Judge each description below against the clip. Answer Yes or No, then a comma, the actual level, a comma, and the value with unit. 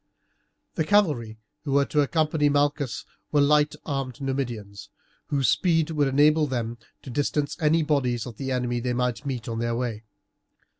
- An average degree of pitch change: Yes, average, 3.6 semitones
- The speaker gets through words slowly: No, average, 160 wpm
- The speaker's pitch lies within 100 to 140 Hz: Yes, low, 135 Hz